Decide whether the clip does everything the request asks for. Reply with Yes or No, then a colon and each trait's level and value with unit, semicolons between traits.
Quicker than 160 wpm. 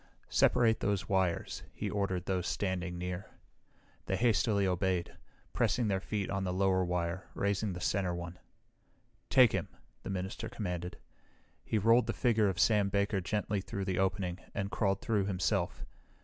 No: average, 155 wpm